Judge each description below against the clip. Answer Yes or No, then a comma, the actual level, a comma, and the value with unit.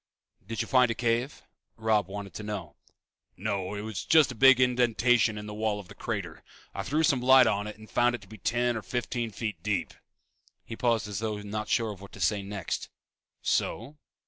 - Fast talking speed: Yes, fast, 210 wpm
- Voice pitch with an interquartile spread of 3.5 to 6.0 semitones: No, average, 2.9 semitones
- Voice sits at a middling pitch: No, low, 110 Hz